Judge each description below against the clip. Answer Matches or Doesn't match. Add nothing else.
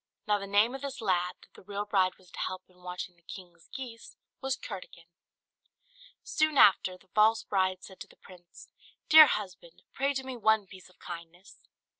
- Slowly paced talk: Doesn't match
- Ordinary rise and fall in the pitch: Matches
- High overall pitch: Matches